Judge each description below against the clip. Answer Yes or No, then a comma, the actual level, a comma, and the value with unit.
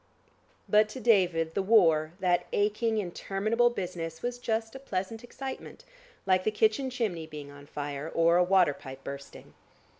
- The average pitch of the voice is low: No, high, 190 Hz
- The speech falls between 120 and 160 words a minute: Yes, average, 155 wpm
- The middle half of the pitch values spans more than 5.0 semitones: Yes, wide, 5.4 semitones